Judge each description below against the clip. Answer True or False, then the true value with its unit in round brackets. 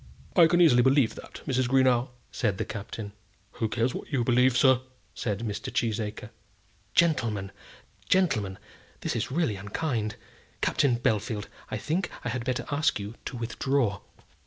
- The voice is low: True (120 Hz)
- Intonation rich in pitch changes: False (4.0 semitones)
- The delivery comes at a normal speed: True (150 wpm)